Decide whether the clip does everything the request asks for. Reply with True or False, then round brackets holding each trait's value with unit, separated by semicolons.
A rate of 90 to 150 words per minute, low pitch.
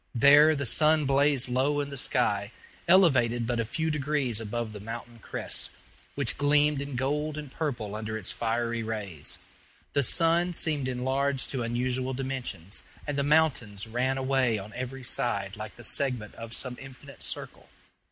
False (160 wpm; 130 Hz)